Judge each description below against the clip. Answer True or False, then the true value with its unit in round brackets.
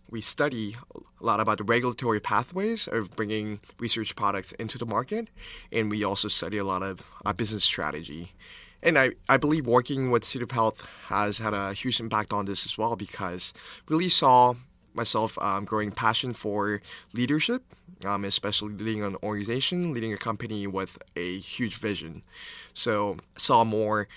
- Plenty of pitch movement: False (3.3 semitones)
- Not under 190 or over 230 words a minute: False (170 wpm)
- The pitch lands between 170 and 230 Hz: False (110 Hz)